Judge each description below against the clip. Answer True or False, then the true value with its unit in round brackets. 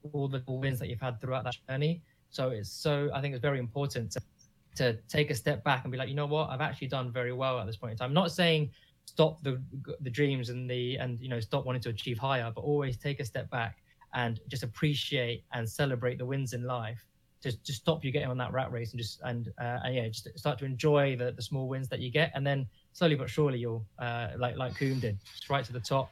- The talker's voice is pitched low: True (130 Hz)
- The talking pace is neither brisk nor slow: False (260 wpm)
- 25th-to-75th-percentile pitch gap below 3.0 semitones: True (2.5 semitones)